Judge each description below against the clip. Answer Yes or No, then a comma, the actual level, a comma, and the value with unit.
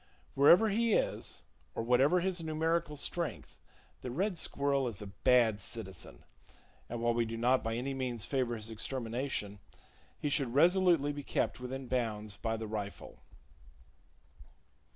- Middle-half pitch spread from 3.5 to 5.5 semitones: Yes, average, 4.5 semitones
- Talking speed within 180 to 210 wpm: No, average, 150 wpm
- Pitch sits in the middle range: No, low, 125 Hz